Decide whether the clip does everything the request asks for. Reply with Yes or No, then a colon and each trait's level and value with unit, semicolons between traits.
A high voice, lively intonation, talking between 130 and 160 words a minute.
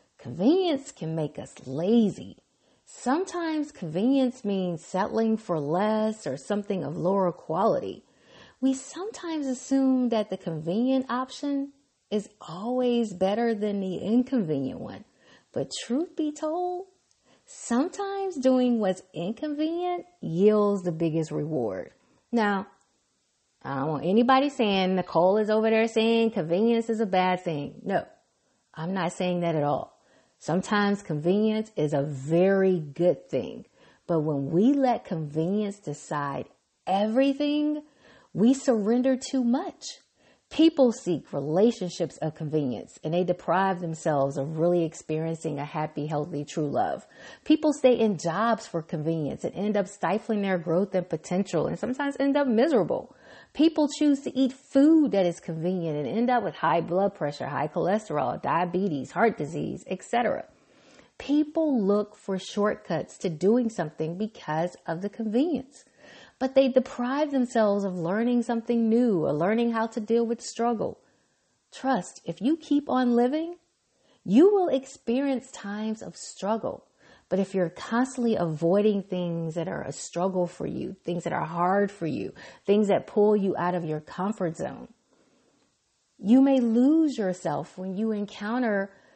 Yes: high, 210 Hz; wide, 6.7 semitones; average, 145 wpm